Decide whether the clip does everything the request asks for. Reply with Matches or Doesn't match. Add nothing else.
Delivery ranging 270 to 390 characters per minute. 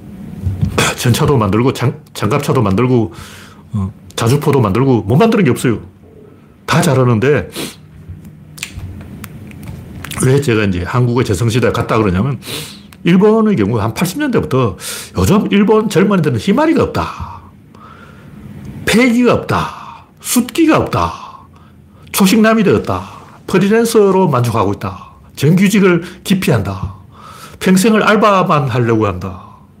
Doesn't match